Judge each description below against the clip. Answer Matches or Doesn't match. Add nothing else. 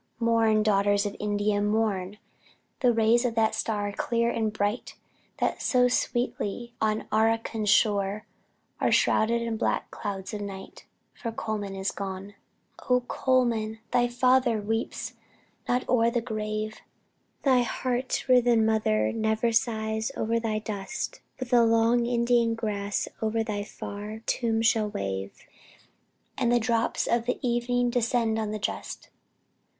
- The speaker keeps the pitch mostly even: Matches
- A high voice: Matches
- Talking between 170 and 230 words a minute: Doesn't match